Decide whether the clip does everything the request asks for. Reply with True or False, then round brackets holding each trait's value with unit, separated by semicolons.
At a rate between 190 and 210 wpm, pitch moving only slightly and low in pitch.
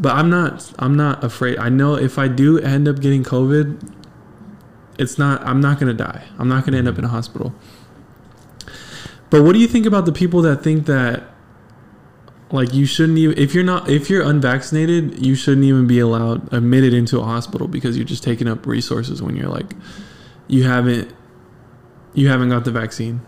False (200 wpm; 3.1 semitones; 130 Hz)